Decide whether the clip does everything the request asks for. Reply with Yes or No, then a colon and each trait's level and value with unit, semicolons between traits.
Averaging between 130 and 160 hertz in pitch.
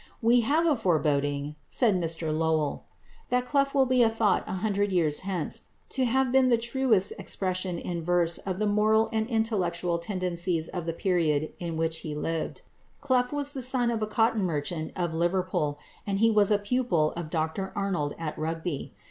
No: medium, 185 Hz